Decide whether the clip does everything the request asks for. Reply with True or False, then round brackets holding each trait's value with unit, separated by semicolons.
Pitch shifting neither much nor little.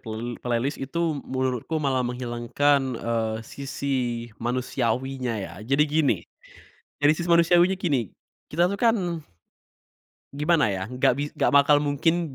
True (3.8 semitones)